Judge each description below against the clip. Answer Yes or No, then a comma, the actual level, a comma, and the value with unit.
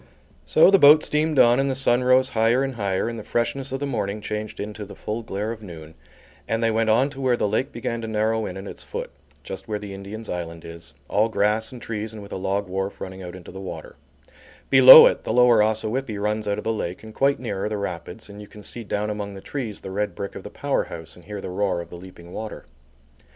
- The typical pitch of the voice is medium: No, low, 105 Hz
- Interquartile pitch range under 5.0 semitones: Yes, average, 3.2 semitones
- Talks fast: Yes, fast, 250 wpm